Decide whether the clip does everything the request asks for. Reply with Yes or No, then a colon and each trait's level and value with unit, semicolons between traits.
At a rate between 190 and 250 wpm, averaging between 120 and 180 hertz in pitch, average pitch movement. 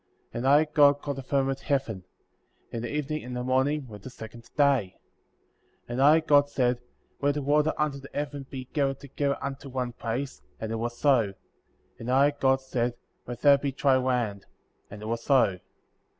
Yes: average, 195 wpm; low, 135 Hz; average, 3.0 semitones